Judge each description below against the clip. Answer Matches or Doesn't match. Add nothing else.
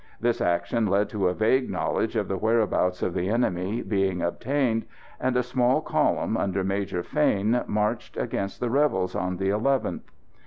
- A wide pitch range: Doesn't match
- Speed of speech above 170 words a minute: Doesn't match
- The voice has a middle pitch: Doesn't match